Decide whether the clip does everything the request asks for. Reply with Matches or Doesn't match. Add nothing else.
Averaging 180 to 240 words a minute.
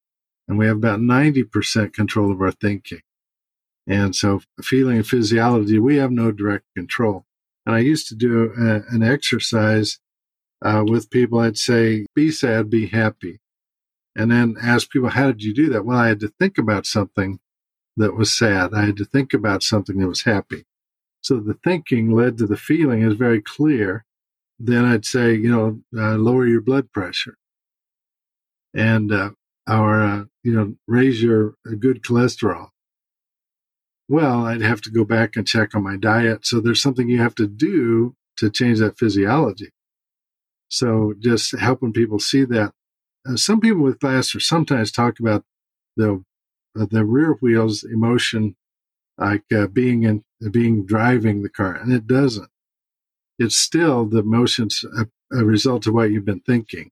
Doesn't match